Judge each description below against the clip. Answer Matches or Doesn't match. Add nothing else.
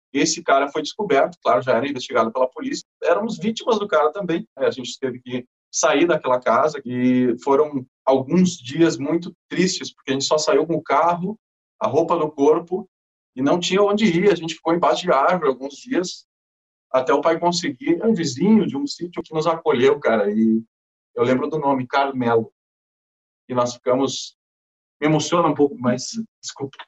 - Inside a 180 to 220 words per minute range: Matches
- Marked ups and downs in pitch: Matches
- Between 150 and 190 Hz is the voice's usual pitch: Matches